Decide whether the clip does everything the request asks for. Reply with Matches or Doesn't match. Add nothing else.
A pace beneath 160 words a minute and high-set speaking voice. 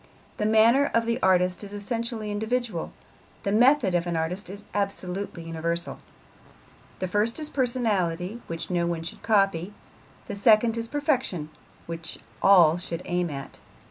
Matches